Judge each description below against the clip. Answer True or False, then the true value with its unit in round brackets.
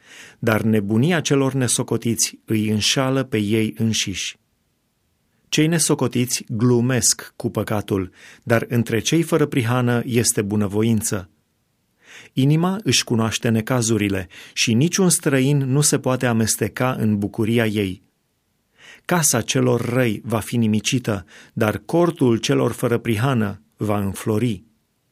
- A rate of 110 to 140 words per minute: True (115 wpm)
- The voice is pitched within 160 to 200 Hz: False (115 Hz)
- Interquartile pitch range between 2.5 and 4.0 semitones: True (3.2 semitones)